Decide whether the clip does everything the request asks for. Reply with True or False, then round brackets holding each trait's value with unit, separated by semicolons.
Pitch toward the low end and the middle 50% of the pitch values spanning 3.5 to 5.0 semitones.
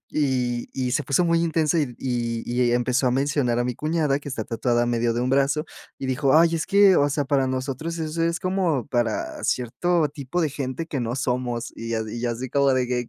True (130 Hz; 3.9 semitones)